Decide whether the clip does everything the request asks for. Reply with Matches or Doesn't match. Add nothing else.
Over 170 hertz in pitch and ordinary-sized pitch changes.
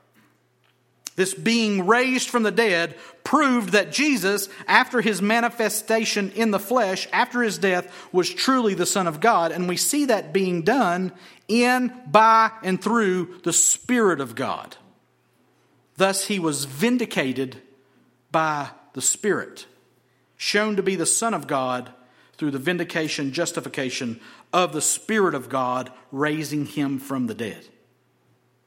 Doesn't match